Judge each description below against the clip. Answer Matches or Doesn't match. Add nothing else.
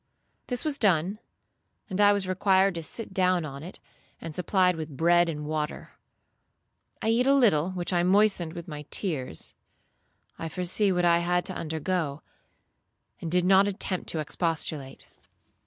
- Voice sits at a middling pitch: Matches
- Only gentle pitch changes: Doesn't match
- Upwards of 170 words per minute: Doesn't match